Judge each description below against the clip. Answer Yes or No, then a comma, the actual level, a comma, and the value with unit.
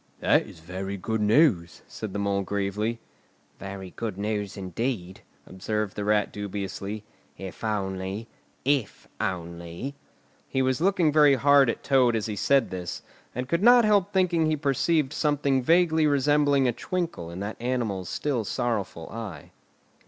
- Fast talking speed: No, average, 145 wpm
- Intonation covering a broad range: Yes, wide, 6.4 semitones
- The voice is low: Yes, low, 110 Hz